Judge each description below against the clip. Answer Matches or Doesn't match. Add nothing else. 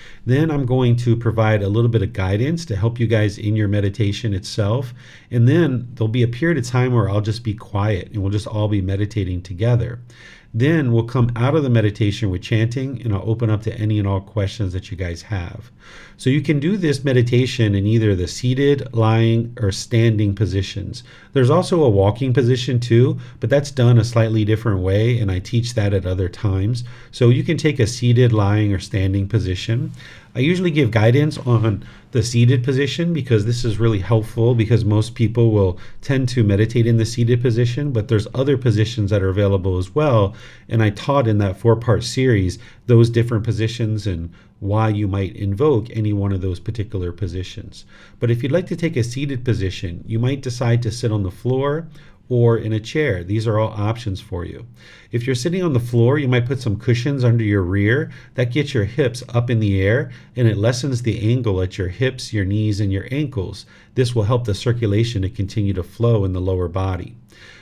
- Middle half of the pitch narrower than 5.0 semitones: Matches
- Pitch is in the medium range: Doesn't match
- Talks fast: Matches